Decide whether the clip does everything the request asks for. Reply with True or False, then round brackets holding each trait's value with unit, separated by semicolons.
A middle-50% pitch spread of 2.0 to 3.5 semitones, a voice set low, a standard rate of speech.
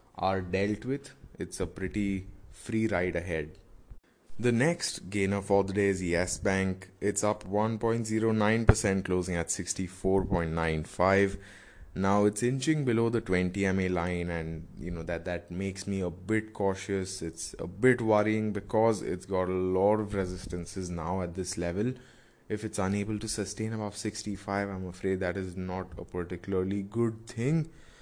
True (2.8 semitones; 95 Hz; 155 wpm)